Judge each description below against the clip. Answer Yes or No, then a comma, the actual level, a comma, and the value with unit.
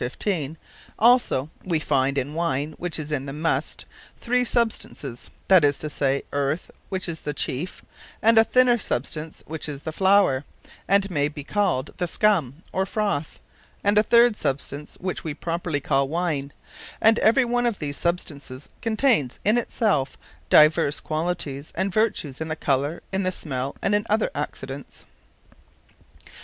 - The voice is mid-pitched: Yes, medium, 160 Hz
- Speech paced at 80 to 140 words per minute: No, average, 160 wpm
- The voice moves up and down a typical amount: No, wide, 6.1 semitones